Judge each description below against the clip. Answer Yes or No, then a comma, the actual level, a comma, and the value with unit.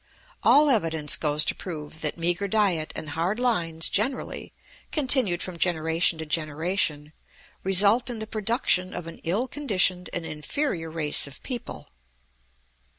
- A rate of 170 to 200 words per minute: No, average, 140 wpm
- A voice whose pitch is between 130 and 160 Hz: No, medium, 175 Hz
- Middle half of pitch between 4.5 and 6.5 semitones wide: Yes, average, 5.2 semitones